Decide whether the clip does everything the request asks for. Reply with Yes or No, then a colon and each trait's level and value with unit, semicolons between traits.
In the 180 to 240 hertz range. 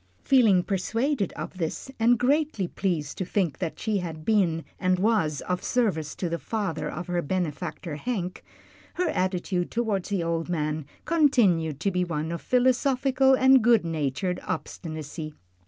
Yes: medium, 185 Hz